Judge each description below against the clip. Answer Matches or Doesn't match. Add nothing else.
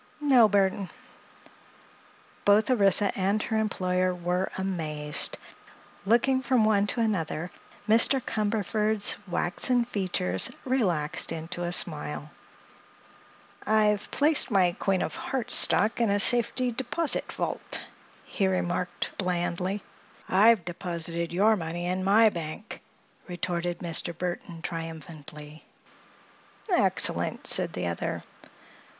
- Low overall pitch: Doesn't match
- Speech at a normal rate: Doesn't match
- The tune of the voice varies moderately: Matches